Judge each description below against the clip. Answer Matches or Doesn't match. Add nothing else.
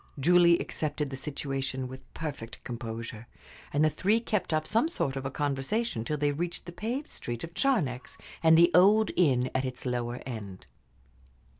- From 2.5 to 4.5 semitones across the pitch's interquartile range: Doesn't match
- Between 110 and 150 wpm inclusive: Doesn't match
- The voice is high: Doesn't match